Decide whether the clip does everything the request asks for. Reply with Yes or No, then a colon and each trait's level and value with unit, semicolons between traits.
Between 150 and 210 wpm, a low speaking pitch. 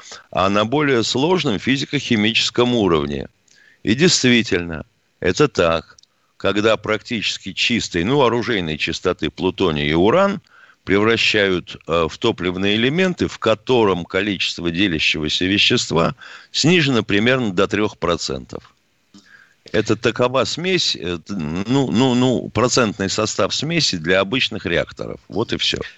No: average, 115 wpm; low, 105 Hz